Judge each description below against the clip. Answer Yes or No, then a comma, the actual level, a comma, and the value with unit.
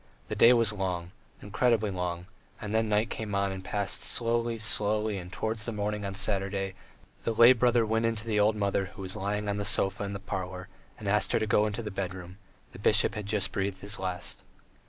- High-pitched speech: No, low, 105 Hz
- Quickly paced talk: Yes, fast, 215 wpm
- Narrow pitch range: Yes, narrow, 2.1 semitones